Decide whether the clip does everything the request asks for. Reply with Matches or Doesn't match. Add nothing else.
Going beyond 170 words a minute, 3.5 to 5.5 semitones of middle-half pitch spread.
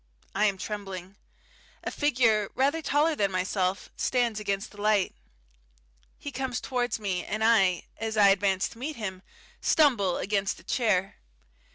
Doesn't match